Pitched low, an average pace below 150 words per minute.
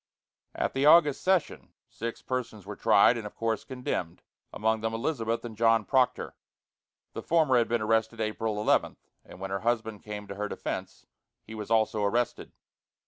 No: low, 115 Hz; average, 170 wpm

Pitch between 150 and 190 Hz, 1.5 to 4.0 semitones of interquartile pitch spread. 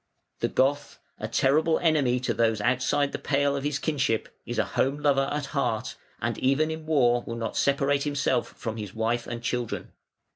No: low, 135 Hz; average, 3.4 semitones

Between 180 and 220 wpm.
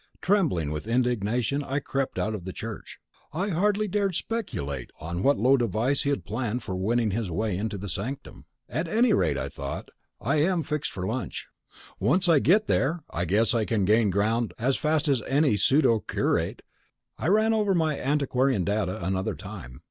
Yes: average, 185 wpm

